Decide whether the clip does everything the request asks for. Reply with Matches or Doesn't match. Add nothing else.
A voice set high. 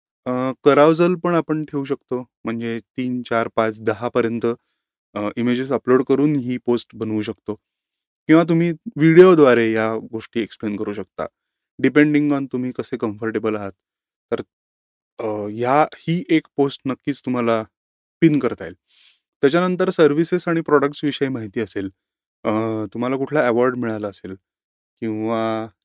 Doesn't match